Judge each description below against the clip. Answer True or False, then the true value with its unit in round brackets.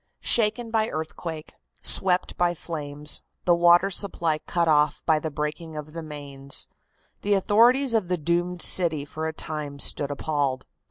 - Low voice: False (160 Hz)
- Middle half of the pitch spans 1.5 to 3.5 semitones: True (3.2 semitones)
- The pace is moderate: True (155 wpm)